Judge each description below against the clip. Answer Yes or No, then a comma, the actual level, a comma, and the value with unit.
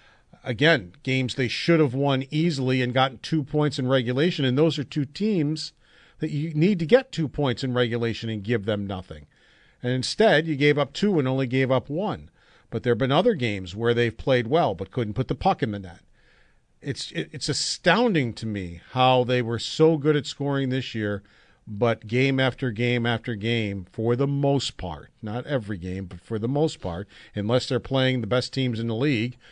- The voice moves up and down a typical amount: Yes, average, 4.1 semitones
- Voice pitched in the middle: No, low, 130 Hz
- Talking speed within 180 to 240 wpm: Yes, fast, 205 wpm